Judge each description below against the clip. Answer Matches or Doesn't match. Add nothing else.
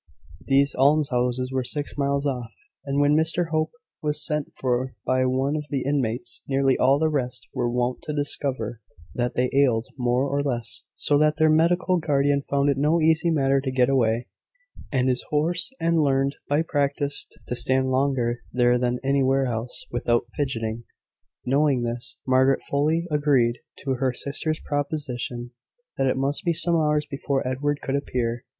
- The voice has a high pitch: Doesn't match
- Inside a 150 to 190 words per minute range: Matches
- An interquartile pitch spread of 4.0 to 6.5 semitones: Doesn't match